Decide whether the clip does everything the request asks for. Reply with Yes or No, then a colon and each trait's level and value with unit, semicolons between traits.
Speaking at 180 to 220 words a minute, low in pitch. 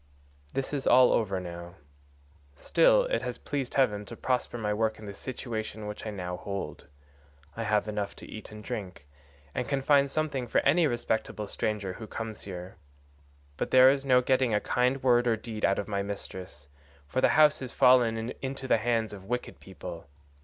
Yes: average, 190 wpm; low, 115 Hz